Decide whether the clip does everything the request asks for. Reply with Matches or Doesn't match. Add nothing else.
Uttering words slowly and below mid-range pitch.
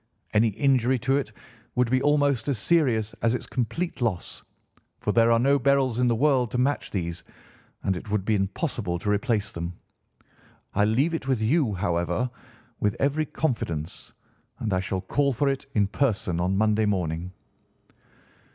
Doesn't match